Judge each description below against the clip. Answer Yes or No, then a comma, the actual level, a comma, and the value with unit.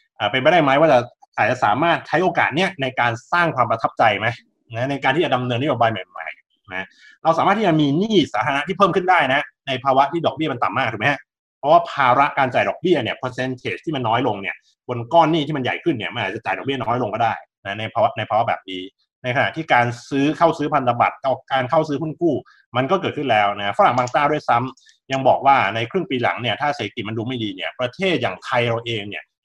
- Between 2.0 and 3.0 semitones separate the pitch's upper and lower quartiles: No, average, 4.4 semitones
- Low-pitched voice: Yes, low, 130 Hz